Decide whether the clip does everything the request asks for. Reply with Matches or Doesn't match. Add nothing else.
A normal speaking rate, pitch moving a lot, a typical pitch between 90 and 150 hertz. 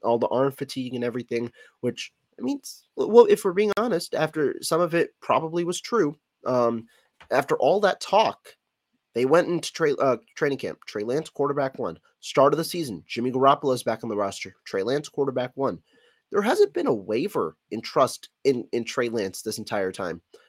Matches